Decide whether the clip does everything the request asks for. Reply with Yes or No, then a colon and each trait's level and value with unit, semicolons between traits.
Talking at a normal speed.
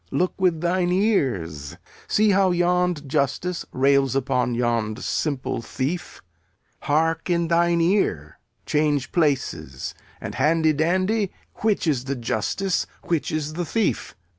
No: slow, 125 wpm